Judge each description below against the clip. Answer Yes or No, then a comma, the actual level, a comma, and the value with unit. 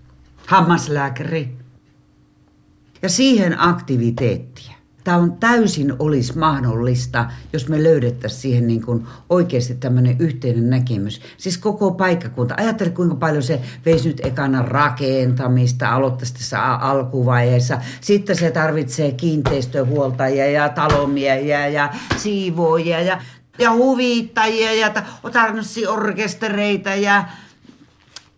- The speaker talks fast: No, average, 100 wpm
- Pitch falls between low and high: Yes, medium, 145 Hz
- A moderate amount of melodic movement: No, wide, 6.7 semitones